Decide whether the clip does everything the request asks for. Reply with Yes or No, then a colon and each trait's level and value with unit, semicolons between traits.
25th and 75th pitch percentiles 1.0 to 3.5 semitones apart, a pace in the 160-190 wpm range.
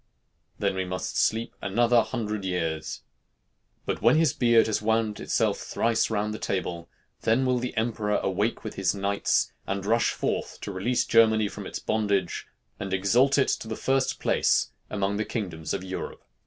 Yes: average, 3.0 semitones; average, 170 wpm